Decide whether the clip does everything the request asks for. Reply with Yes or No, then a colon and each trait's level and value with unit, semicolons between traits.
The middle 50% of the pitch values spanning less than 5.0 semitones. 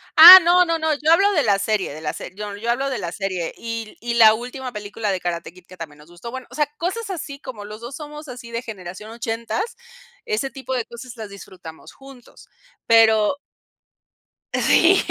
No: wide, 5.5 semitones